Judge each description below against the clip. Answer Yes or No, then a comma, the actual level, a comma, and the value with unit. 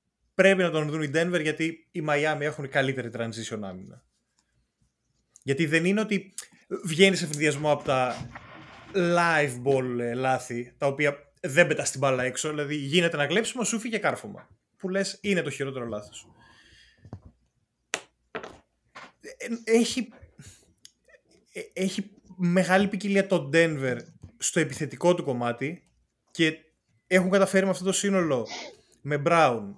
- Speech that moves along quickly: No, average, 130 wpm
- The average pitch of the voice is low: No, medium, 155 Hz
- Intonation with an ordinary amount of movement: No, wide, 5.8 semitones